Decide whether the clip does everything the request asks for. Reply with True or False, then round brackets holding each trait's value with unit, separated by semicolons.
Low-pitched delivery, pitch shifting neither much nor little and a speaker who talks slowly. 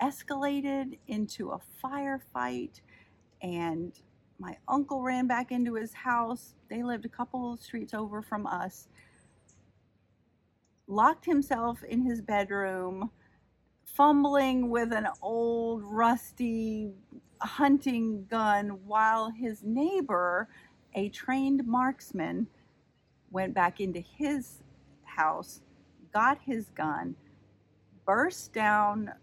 False (230 Hz; 4.5 semitones; 100 wpm)